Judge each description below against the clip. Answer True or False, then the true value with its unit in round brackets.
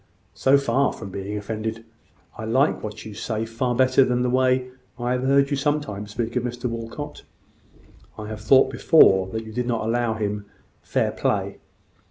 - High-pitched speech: False (120 Hz)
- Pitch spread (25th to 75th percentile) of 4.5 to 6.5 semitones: False (3.0 semitones)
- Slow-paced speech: False (185 wpm)